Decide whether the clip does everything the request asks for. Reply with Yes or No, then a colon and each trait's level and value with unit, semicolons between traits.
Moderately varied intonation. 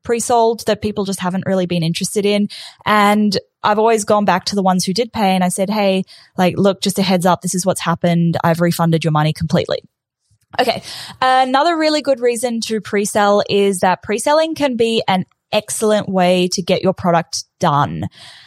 Yes: average, 3.6 semitones